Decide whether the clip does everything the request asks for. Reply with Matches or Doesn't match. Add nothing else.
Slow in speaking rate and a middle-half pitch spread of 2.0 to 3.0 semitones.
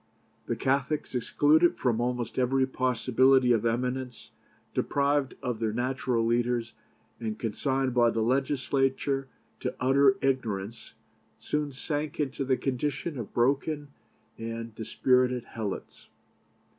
Matches